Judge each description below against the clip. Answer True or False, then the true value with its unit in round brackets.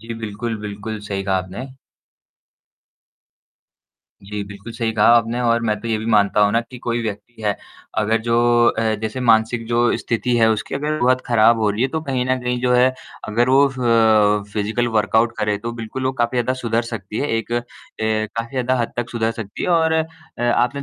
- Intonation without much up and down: True (2.2 semitones)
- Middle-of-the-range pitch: False (115 Hz)